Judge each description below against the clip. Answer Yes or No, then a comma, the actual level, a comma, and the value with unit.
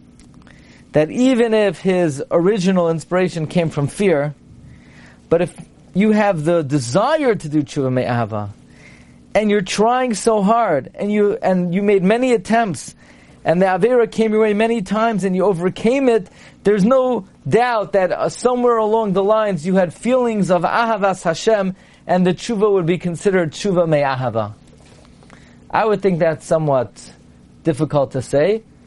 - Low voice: No, high, 190 Hz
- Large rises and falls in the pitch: Yes, wide, 5.7 semitones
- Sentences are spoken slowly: No, average, 155 wpm